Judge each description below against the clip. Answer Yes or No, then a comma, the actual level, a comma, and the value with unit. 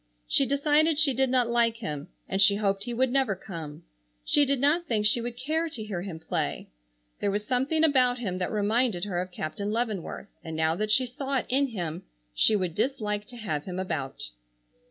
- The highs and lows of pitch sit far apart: Yes, wide, 5.8 semitones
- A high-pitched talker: Yes, high, 220 Hz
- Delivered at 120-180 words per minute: No, fast, 205 wpm